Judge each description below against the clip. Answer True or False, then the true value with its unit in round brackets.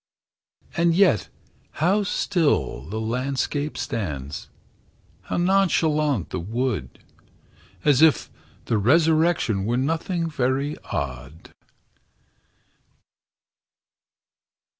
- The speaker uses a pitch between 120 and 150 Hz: True (135 Hz)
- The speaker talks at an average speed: False (75 wpm)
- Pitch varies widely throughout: True (7.8 semitones)